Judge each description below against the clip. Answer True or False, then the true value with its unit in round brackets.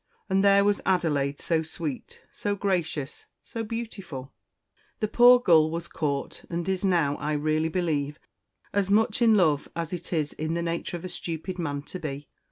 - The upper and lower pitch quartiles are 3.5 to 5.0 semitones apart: True (4.3 semitones)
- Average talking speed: True (175 wpm)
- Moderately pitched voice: True (170 Hz)